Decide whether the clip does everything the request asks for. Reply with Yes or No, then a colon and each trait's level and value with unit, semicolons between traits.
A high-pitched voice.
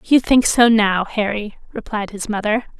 Yes: high, 215 Hz